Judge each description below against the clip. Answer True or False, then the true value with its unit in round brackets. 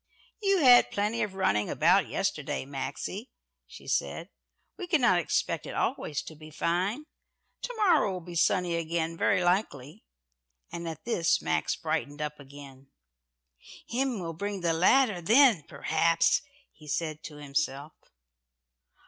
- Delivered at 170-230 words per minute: False (140 wpm)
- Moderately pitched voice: True (170 Hz)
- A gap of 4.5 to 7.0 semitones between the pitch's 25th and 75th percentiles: True (5.5 semitones)